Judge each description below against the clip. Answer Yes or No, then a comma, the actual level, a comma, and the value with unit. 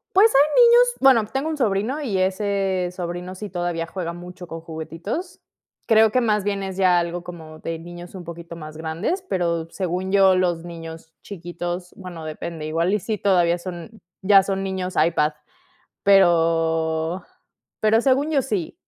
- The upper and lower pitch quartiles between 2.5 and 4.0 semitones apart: Yes, average, 3.4 semitones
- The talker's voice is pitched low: No, medium, 180 Hz